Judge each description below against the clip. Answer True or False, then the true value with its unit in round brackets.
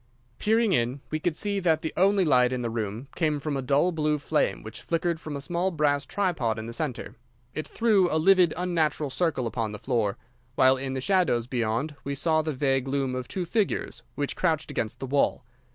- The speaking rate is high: True (210 wpm)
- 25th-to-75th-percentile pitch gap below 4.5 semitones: False (5.1 semitones)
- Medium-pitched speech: True (150 Hz)